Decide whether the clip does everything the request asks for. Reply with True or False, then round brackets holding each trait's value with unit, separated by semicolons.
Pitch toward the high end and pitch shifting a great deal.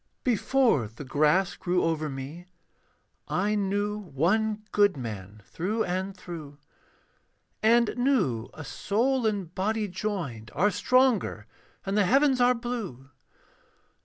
True (195 Hz; 6.4 semitones)